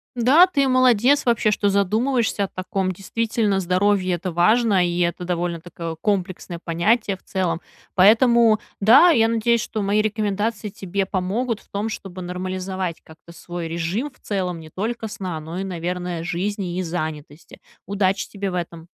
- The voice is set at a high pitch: Yes, high, 195 Hz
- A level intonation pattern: No, average, 3.8 semitones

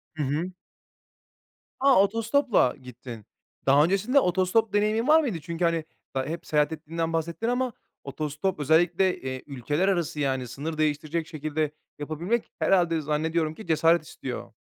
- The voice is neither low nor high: Yes, medium, 165 Hz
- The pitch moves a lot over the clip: No, average, 4.4 semitones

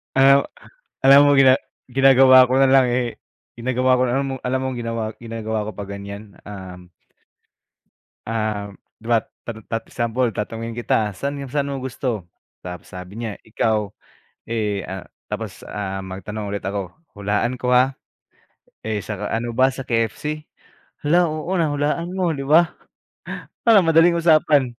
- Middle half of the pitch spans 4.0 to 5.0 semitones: Yes, average, 4.4 semitones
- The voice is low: Yes, low, 120 Hz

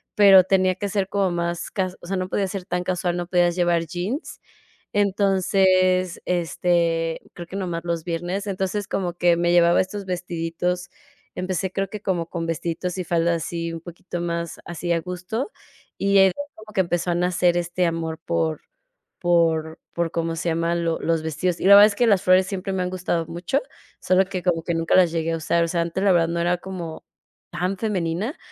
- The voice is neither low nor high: Yes, medium, 175 Hz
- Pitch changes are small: Yes, narrow, 1.9 semitones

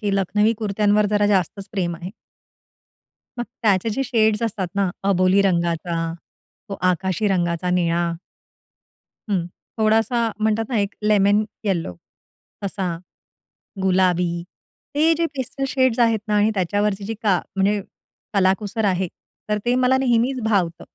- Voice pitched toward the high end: Yes, high, 205 Hz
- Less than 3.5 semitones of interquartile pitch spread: Yes, average, 3.1 semitones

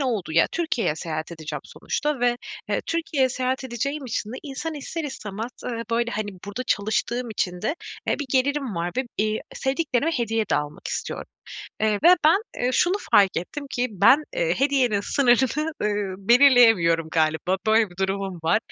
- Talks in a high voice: Yes, high, 235 Hz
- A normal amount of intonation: No, wide, 5.9 semitones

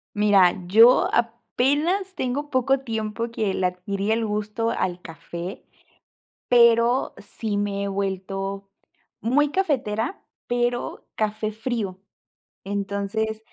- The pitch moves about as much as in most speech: Yes, average, 3.4 semitones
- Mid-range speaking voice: No, high, 220 Hz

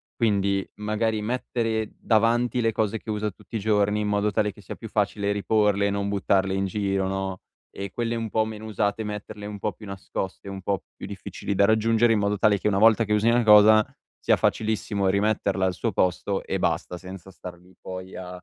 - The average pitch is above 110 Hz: No, low, 105 Hz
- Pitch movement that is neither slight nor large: No, narrow, 1.9 semitones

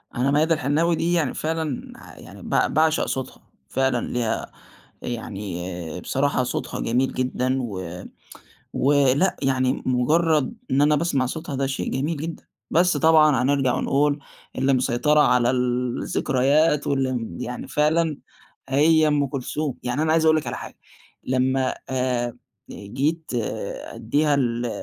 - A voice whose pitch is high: No, low, 135 Hz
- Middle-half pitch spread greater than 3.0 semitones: Yes, average, 3.4 semitones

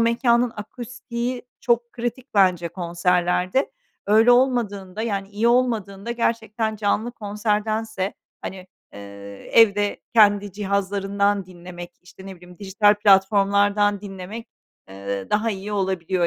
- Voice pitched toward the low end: No, high, 205 Hz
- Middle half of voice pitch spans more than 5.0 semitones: No, average, 3.1 semitones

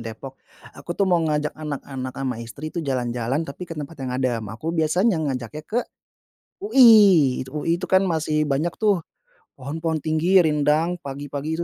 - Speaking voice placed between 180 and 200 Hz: No, medium, 155 Hz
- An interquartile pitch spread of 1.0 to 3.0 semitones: No, average, 3.9 semitones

